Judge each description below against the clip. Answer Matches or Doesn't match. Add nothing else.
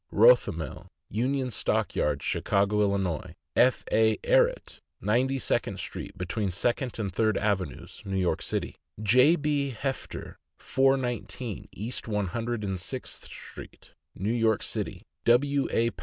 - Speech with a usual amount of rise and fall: Matches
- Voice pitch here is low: Matches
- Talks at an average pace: Doesn't match